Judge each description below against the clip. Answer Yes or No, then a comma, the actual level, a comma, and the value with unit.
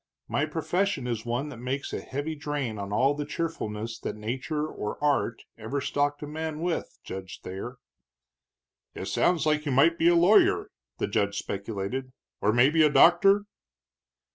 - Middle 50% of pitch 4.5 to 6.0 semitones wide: Yes, wide, 5.5 semitones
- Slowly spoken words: No, average, 165 wpm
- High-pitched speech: No, medium, 140 Hz